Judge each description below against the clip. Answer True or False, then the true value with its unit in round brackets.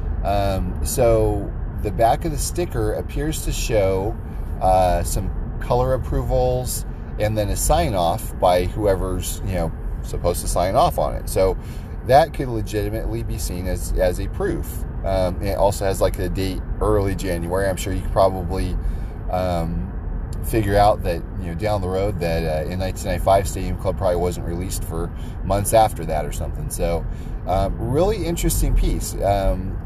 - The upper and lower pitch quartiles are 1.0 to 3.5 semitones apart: True (3.1 semitones)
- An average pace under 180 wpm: True (165 wpm)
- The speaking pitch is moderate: False (95 Hz)